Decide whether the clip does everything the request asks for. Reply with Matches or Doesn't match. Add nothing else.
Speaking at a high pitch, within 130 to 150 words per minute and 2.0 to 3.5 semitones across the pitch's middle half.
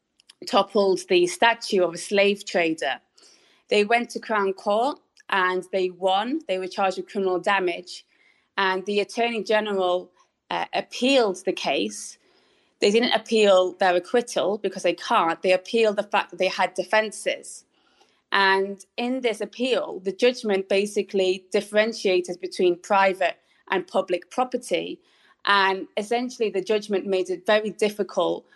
Matches